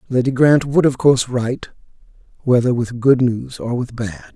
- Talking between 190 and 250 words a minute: No, average, 180 wpm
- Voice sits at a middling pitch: No, low, 125 Hz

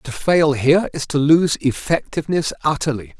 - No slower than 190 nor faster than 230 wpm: No, average, 150 wpm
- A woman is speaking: No, male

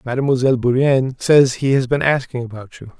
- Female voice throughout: No, male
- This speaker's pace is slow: No, average, 180 wpm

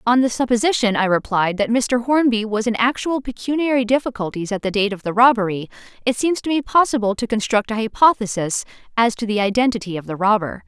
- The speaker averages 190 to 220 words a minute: Yes, average, 195 wpm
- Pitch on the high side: Yes, high, 225 Hz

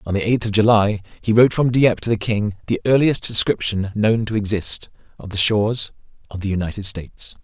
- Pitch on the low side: Yes, low, 105 Hz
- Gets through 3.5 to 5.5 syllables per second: No, 5.7 syllables/s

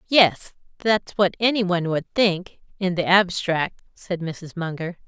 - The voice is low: No, medium, 185 Hz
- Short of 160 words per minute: Yes, average, 140 wpm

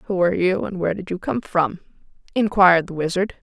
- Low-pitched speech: No, medium, 185 Hz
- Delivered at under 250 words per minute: Yes, fast, 205 wpm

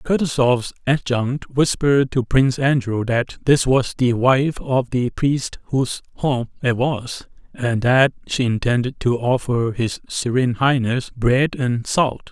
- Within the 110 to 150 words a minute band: Yes, average, 145 wpm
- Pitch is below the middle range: Yes, low, 125 Hz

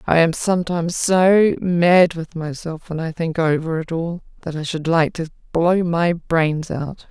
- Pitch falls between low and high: Yes, medium, 165 Hz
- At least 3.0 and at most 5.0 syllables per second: Yes, 4.2 syllables/s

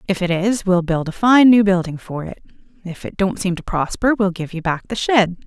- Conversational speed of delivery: No, fast, 250 wpm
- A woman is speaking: Yes, female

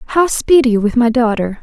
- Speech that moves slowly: No, fast, 220 wpm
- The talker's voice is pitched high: Yes, high, 245 Hz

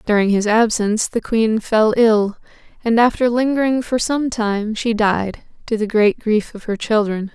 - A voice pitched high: Yes, high, 220 Hz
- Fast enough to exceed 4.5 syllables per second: No, 4.4 syllables/s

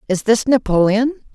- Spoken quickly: No, slow, 135 wpm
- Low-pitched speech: No, high, 225 Hz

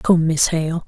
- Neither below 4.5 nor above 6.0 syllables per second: No, 3.7 syllables/s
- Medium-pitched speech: Yes, medium, 165 Hz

